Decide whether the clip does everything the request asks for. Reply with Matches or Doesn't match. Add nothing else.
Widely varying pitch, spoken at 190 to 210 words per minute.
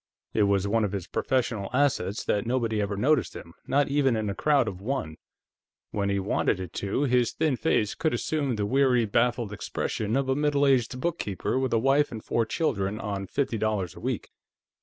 Doesn't match